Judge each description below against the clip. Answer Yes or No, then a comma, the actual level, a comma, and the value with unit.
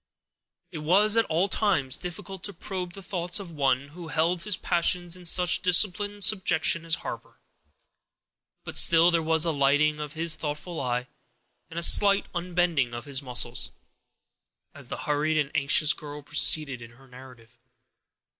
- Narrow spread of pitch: No, average, 3.8 semitones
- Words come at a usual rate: Yes, average, 160 wpm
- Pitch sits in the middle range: Yes, medium, 160 Hz